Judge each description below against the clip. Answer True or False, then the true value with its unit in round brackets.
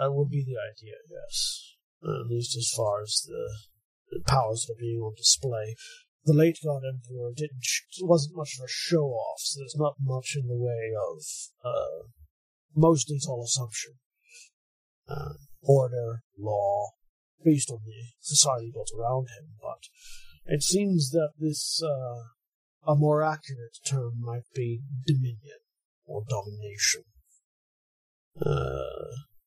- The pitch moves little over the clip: False (4.5 semitones)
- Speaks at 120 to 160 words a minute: True (145 wpm)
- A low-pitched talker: True (130 Hz)